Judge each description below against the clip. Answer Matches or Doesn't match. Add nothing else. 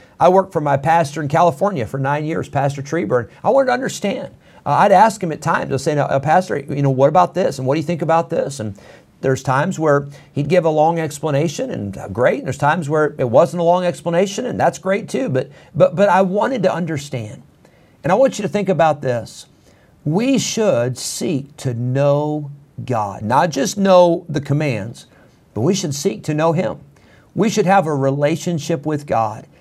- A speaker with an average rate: Doesn't match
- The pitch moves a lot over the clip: Doesn't match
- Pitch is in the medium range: Matches